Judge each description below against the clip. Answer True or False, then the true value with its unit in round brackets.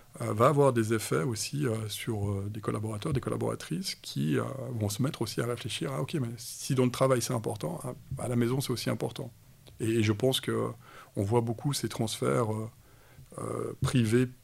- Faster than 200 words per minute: False (175 wpm)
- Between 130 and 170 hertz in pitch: False (120 Hz)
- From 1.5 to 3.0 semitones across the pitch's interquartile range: True (2.4 semitones)